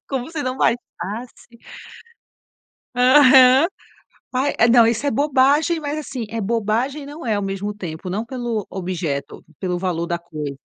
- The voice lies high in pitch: Yes, high, 235 Hz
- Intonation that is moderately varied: No, wide, 5.8 semitones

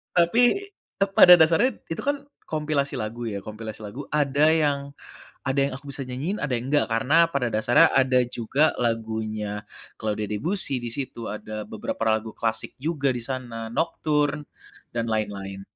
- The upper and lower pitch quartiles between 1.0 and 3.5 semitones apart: No, average, 5.2 semitones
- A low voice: Yes, low, 130 Hz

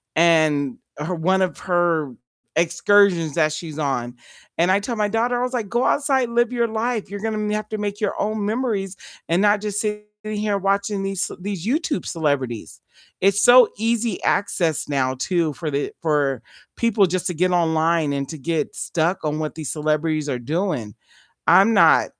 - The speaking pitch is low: No, medium, 185 Hz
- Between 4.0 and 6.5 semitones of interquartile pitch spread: Yes, average, 5.2 semitones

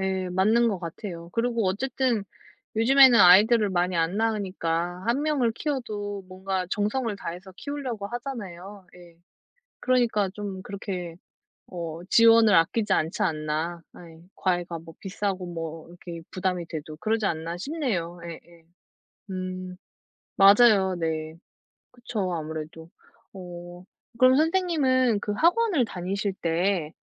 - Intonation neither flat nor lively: Yes, average, 4.8 semitones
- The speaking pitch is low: No, high, 190 Hz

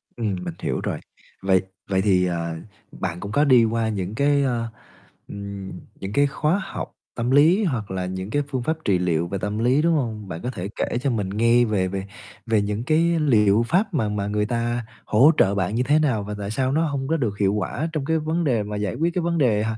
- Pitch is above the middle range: No, low, 110 Hz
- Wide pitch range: Yes, wide, 6.0 semitones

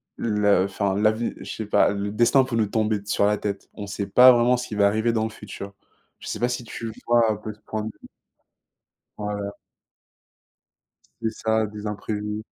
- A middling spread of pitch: No, narrow, 1.7 semitones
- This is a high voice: No, low, 105 Hz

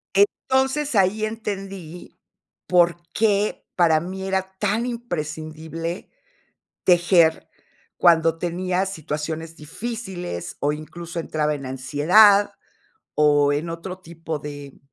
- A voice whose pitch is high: No, medium, 170 Hz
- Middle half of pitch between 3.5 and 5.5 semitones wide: Yes, average, 4.0 semitones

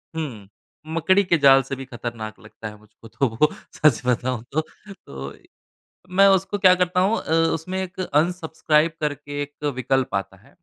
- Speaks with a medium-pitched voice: Yes, medium, 145 Hz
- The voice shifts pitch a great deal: Yes, wide, 6.9 semitones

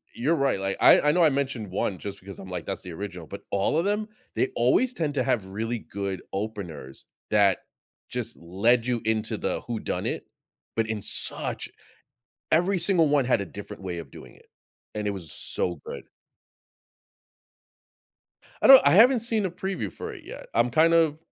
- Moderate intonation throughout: No, wide, 8.1 semitones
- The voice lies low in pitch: Yes, low, 115 Hz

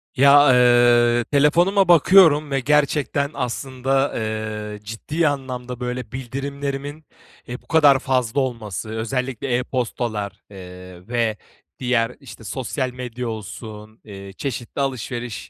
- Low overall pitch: Yes, low, 125 Hz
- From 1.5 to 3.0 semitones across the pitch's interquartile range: No, average, 3.7 semitones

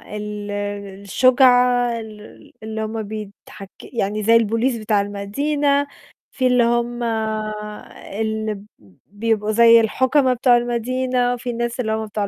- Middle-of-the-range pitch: No, high, 230 Hz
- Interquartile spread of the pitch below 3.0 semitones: Yes, narrow, 2.6 semitones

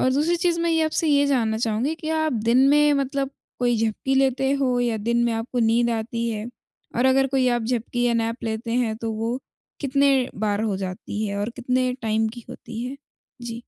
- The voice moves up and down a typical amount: Yes, average, 3.2 semitones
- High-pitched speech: Yes, high, 240 Hz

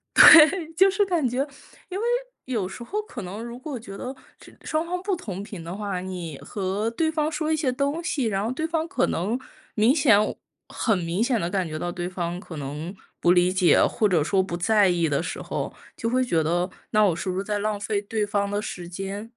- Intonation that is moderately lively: No, wide, 7.1 semitones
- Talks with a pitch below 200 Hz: No, high, 205 Hz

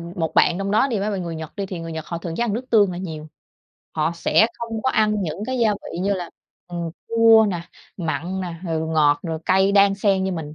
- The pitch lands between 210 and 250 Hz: No, medium, 185 Hz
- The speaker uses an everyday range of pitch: Yes, average, 3.9 semitones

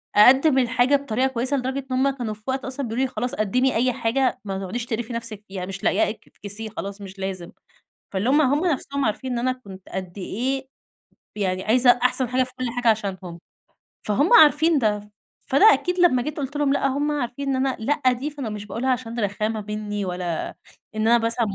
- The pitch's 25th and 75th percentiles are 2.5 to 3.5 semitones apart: No, average, 4.1 semitones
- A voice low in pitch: No, high, 245 Hz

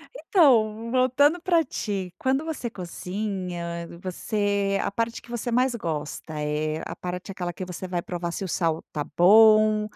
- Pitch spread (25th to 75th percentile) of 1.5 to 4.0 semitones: No, average, 5.0 semitones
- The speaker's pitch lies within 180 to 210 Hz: Yes, high, 200 Hz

